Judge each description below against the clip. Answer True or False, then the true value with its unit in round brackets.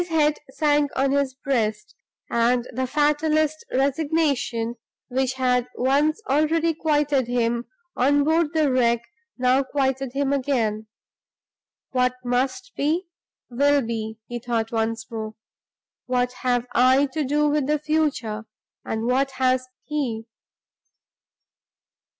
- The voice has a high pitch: True (265 Hz)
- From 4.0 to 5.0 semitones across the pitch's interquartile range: False (3.5 semitones)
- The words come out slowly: True (120 wpm)